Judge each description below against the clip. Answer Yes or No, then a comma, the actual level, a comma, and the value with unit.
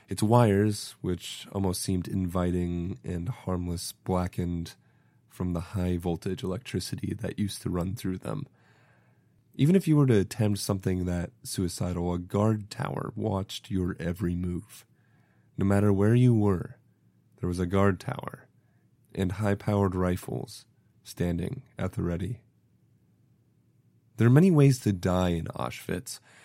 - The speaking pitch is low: Yes, low, 100 Hz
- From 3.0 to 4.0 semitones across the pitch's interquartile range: No, average, 4.8 semitones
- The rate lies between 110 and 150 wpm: Yes, average, 140 wpm